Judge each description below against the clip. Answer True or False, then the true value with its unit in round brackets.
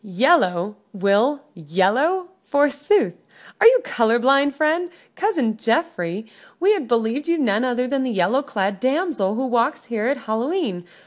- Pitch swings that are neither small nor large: False (5.9 semitones)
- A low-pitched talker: False (250 Hz)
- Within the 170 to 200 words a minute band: False (150 wpm)